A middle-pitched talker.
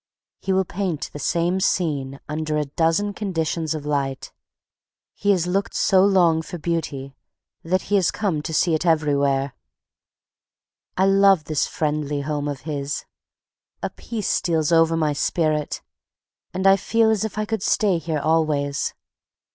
Yes: medium, 165 Hz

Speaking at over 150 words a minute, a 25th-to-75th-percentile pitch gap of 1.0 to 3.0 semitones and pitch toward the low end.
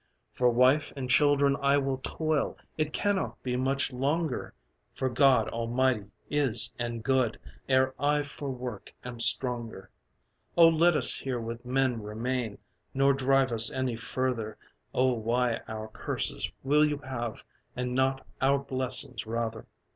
No: average, 145 wpm; average, 2.7 semitones; low, 130 Hz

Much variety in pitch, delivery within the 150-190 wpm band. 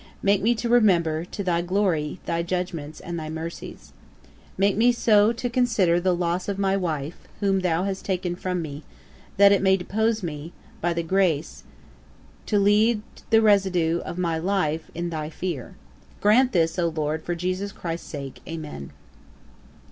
No: average, 3.5 semitones; average, 165 wpm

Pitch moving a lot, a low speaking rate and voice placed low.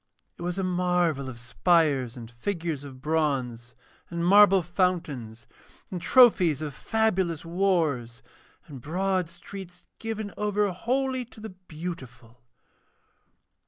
No: wide, 5.9 semitones; slow, 120 wpm; medium, 170 Hz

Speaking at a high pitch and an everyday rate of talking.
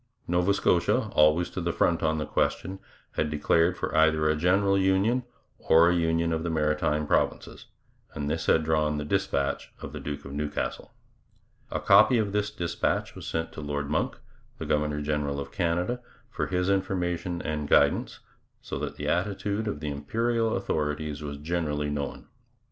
No: very low, 80 Hz; average, 170 wpm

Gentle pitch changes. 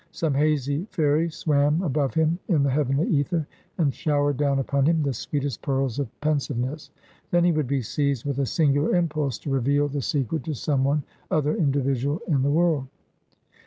Yes: narrow, 2.1 semitones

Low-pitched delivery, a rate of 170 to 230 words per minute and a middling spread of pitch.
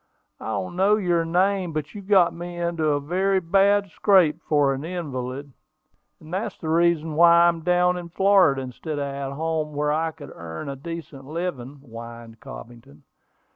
No: medium, 160 Hz; average, 175 wpm; average, 4.3 semitones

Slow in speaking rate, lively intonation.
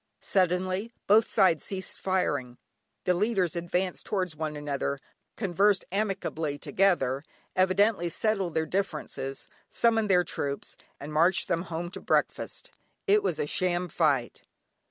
No: slow, 130 wpm; average, 3.8 semitones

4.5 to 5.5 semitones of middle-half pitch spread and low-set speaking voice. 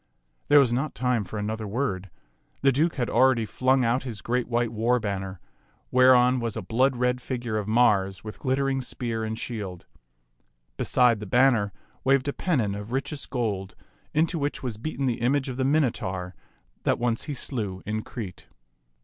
No: average, 3.6 semitones; low, 120 Hz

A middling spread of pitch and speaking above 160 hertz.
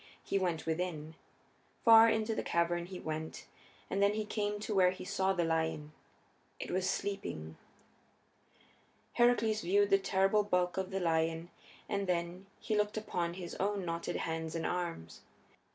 Yes: average, 3.3 semitones; medium, 185 Hz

